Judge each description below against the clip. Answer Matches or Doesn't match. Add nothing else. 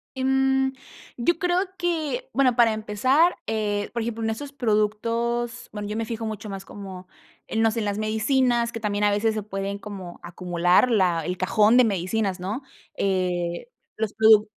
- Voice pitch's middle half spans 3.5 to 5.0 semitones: Doesn't match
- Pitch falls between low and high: Doesn't match